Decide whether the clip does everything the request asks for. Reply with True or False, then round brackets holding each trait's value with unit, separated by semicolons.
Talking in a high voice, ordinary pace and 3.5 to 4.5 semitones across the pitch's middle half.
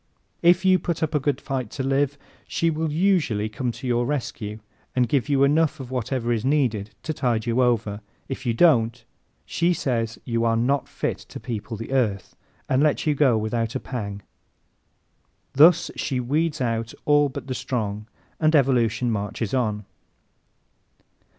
False (125 Hz; 170 wpm; 4.2 semitones)